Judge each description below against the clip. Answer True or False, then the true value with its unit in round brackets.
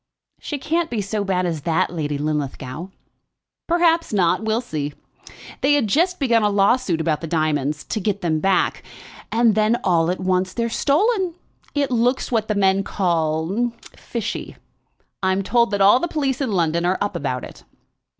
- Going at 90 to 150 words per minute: False (175 wpm)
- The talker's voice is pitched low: False (200 Hz)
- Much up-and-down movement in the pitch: True (6.3 semitones)